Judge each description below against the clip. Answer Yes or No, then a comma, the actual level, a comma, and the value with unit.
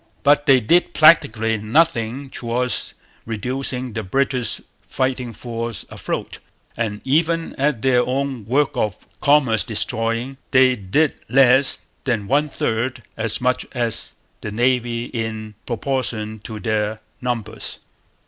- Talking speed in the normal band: No, slow, 120 wpm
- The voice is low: Yes, low, 125 Hz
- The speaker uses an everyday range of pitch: Yes, average, 3.2 semitones